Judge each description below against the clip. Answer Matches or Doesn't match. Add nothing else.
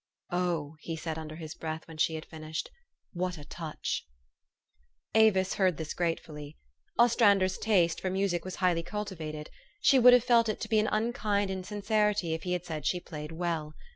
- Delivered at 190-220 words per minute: Matches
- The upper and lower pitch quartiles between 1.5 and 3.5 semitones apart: Doesn't match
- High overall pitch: Doesn't match